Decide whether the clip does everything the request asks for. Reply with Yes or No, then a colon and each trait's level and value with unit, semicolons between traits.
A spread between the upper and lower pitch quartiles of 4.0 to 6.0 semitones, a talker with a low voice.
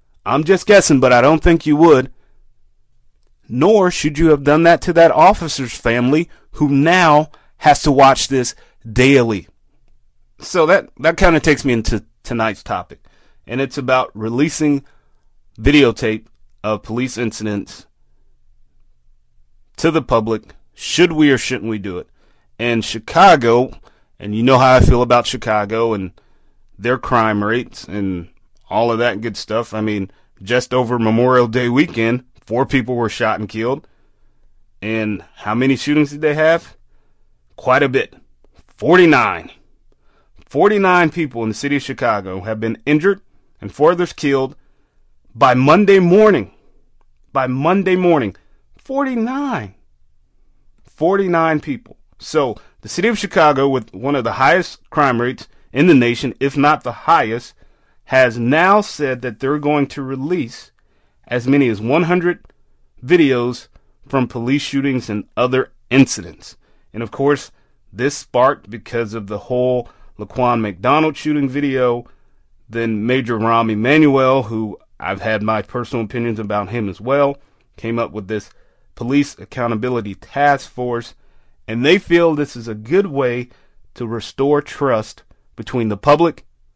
Yes: average, 4.8 semitones; low, 125 Hz